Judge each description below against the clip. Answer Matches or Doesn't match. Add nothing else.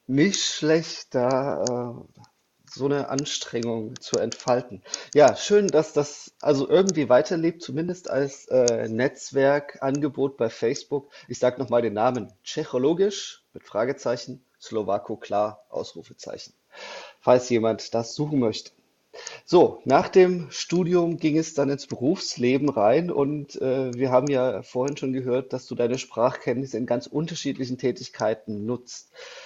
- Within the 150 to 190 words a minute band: Doesn't match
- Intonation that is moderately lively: Matches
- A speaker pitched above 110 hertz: Matches